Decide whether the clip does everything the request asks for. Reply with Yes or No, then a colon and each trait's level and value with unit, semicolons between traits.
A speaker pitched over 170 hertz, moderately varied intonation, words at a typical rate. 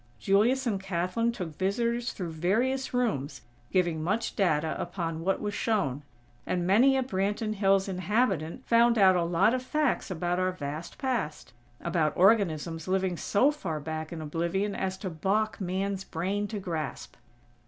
Yes: high, 190 Hz; average, 4.4 semitones; average, 155 wpm